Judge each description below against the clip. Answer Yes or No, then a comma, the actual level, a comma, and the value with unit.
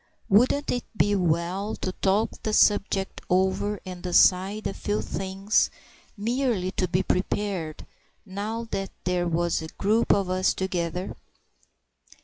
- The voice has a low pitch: No, high, 190 Hz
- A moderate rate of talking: No, slow, 125 wpm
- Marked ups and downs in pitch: No, narrow, 2.4 semitones